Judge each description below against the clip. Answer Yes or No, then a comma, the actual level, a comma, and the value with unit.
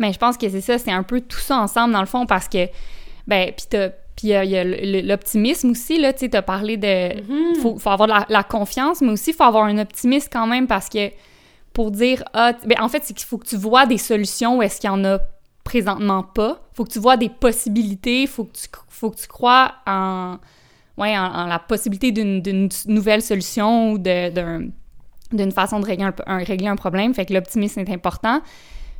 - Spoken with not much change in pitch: No, average, 3.6 semitones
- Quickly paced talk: Yes, fast, 225 wpm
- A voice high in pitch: Yes, high, 215 Hz